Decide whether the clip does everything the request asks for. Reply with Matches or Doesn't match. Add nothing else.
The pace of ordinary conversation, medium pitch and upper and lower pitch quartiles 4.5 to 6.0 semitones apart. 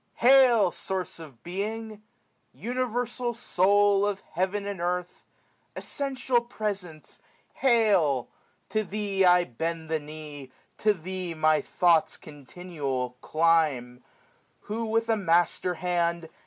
Doesn't match